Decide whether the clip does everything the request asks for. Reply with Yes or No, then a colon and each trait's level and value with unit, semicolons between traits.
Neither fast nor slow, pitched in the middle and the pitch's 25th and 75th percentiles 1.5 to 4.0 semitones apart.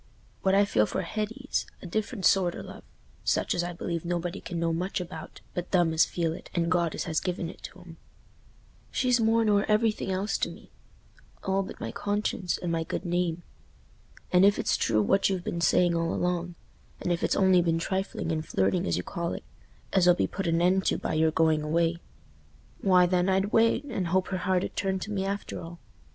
No: fast, 210 wpm; medium, 180 Hz; narrow, 2.5 semitones